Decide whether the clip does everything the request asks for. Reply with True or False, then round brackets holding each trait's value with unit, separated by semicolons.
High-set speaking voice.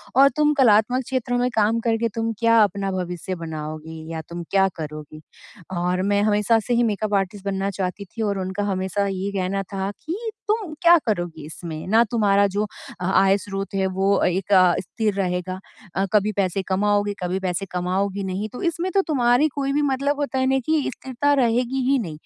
True (200 Hz)